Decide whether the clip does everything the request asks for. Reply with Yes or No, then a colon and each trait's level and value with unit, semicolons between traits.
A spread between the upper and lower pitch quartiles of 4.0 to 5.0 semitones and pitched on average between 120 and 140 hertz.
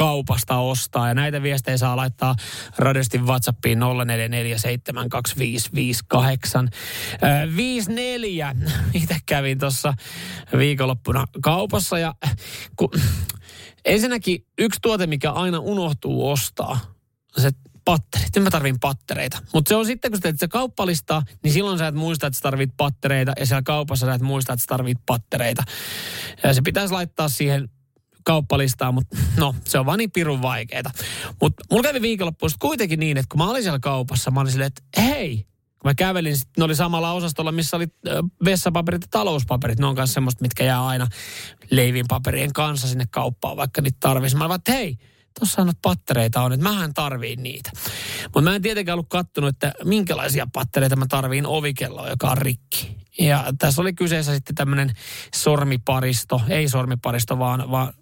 Yes: average, 4.5 semitones; low, 135 Hz